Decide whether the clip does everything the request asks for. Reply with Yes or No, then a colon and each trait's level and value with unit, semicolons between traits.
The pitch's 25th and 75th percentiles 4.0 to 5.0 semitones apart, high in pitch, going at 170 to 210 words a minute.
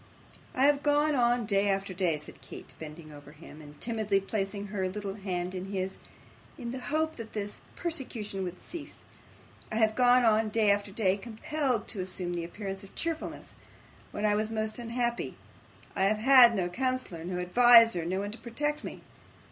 Yes: average, 4.3 semitones; high, 210 Hz; average, 180 wpm